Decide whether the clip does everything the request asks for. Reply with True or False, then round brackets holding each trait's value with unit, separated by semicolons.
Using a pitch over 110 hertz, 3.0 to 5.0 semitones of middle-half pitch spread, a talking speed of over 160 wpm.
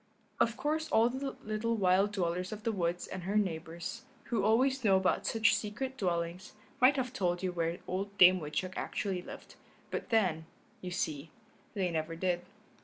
True (190 Hz; 4.1 semitones; 175 wpm)